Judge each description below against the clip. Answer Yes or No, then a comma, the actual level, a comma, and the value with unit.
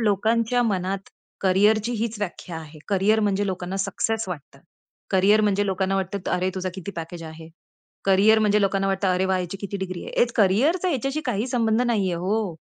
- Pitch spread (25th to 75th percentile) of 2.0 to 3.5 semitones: Yes, average, 2.8 semitones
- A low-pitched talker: No, high, 195 Hz